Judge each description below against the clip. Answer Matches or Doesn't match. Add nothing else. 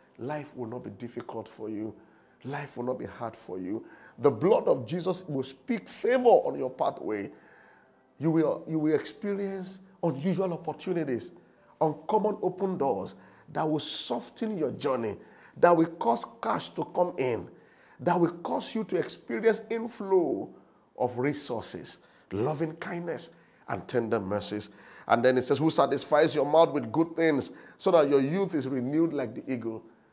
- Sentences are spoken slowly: Doesn't match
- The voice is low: Doesn't match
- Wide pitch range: Matches